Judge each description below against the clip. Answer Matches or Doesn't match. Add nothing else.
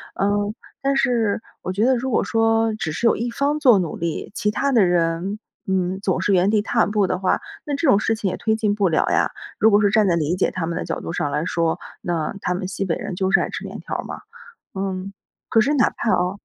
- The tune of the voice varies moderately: Matches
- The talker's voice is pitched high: Matches